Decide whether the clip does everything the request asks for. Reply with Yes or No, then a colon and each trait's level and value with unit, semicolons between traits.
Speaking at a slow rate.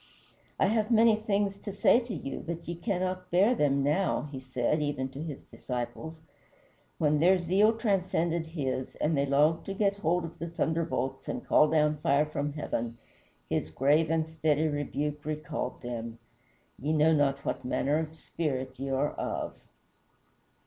No: average, 165 wpm